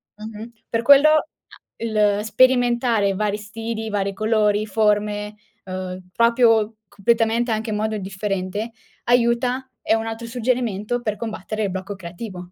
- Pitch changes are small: Yes, narrow, 2.3 semitones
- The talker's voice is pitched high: Yes, high, 220 Hz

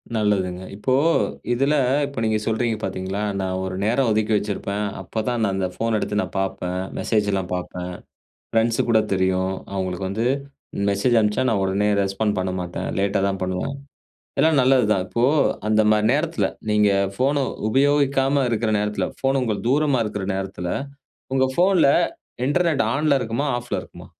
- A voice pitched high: No, low, 110 Hz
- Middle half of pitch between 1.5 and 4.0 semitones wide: No, average, 5.1 semitones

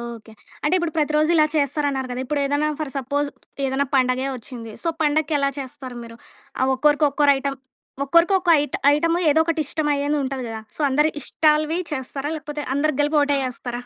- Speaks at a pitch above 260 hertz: Yes, very high, 285 Hz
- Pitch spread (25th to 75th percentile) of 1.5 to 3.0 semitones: Yes, narrow, 2.5 semitones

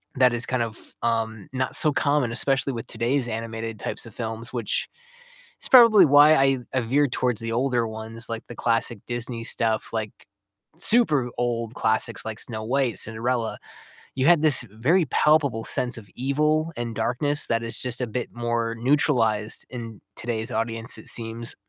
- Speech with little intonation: No, average, 3.0 semitones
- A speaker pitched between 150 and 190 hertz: No, low, 120 Hz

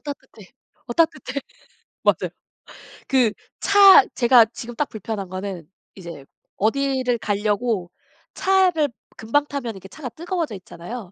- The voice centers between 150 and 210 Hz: No, high, 240 Hz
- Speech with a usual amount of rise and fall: No, wide, 6.0 semitones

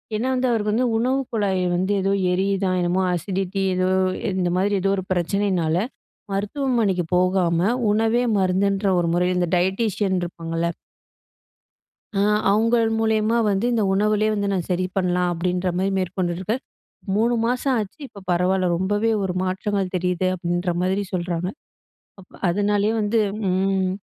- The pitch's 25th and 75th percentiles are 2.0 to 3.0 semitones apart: Yes, narrow, 2.5 semitones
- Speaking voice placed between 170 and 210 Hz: Yes, high, 190 Hz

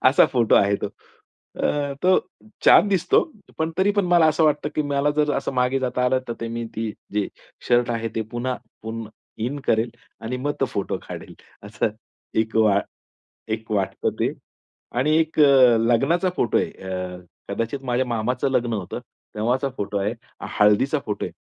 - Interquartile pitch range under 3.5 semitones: No, average, 4.2 semitones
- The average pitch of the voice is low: Yes, low, 125 Hz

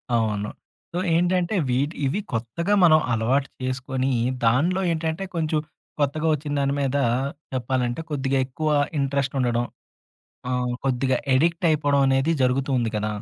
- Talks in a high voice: No, low, 135 Hz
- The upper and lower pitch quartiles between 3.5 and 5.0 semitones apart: Yes, average, 3.8 semitones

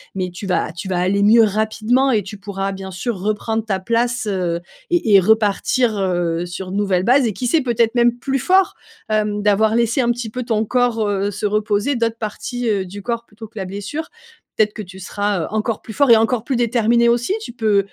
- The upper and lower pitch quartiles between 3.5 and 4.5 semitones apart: No, average, 3.1 semitones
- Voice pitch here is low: No, high, 215 Hz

